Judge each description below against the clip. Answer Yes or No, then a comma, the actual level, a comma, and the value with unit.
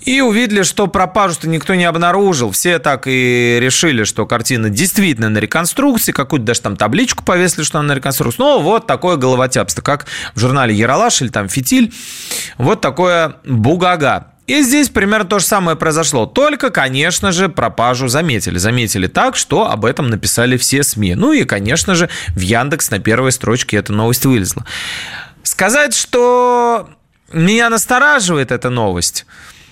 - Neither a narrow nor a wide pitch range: No, wide, 8.7 semitones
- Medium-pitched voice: Yes, medium, 150 Hz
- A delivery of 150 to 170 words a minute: Yes, average, 155 wpm